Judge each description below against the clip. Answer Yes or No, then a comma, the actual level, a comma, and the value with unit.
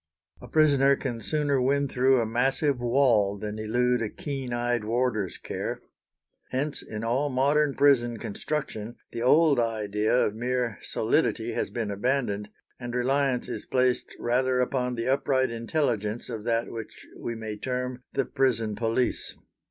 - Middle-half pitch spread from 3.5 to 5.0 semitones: No, average, 2.8 semitones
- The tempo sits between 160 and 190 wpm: No, average, 150 wpm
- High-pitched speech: No, low, 125 Hz